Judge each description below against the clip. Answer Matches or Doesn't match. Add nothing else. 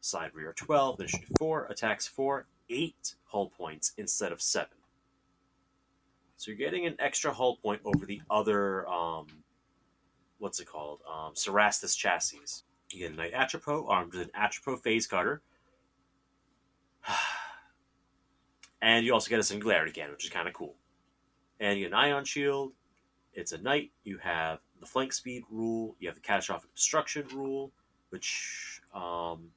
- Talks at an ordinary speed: Matches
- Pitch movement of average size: Doesn't match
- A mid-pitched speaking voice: Doesn't match